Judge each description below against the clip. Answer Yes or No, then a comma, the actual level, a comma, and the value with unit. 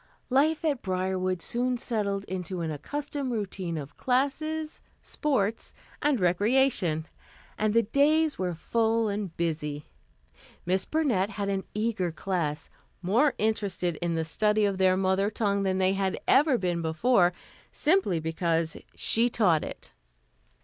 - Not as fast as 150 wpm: Yes, slow, 135 wpm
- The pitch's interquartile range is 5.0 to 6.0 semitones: Yes, wide, 5.4 semitones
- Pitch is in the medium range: No, high, 200 Hz